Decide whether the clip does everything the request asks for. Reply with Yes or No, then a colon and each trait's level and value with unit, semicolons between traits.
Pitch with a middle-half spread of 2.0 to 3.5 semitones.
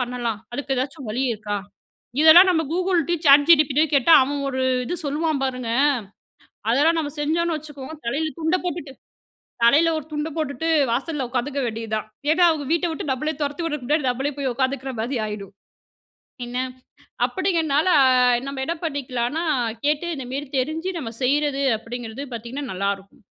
No: average, 4.1 semitones